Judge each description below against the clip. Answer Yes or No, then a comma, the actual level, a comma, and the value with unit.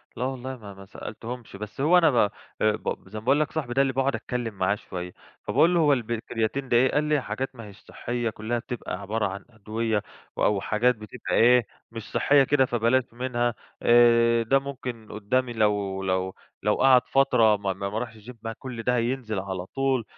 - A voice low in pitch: Yes, low, 115 Hz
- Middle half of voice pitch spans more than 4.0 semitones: No, average, 3.4 semitones